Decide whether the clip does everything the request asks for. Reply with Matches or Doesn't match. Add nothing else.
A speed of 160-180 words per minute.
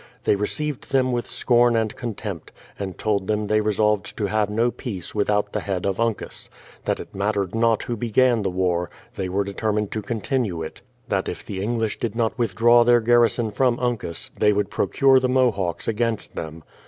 Doesn't match